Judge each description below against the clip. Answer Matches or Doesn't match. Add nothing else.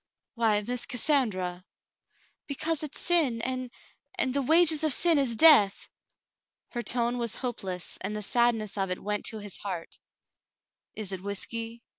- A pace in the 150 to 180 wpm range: Matches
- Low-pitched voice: Doesn't match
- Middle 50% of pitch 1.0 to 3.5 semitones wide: Doesn't match